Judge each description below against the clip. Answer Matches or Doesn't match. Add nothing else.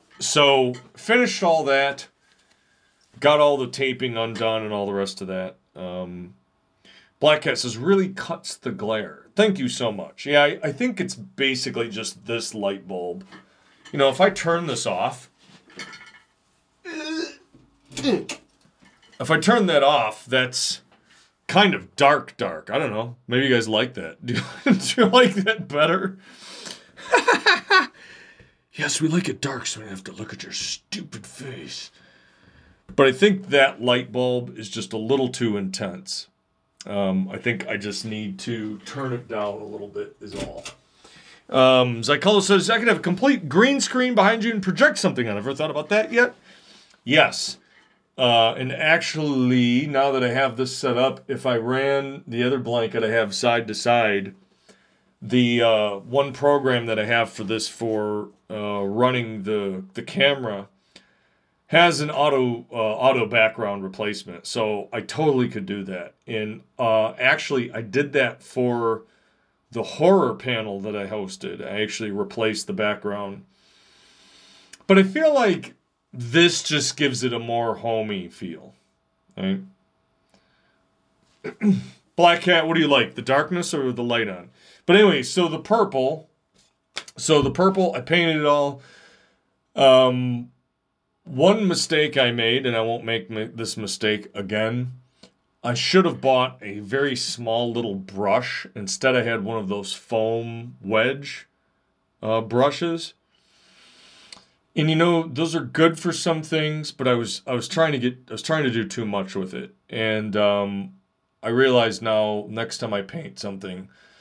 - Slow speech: Doesn't match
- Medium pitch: Doesn't match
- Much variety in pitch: Matches